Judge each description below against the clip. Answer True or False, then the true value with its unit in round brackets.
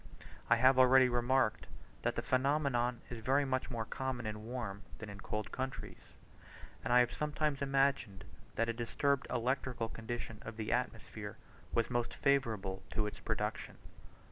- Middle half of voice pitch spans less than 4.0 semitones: True (2.9 semitones)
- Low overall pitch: True (120 Hz)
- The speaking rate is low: False (155 wpm)